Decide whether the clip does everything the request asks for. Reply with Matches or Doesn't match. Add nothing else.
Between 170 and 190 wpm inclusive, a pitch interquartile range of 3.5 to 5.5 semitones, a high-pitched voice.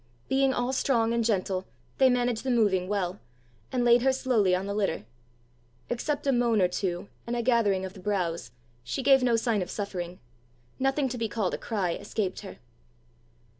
Matches